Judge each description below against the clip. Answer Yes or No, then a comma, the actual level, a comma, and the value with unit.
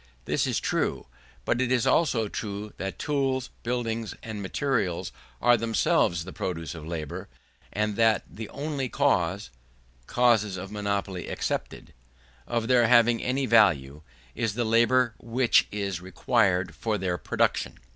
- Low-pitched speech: Yes, low, 110 Hz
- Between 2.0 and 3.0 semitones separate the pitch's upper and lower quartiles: No, average, 4.1 semitones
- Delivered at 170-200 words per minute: No, average, 140 wpm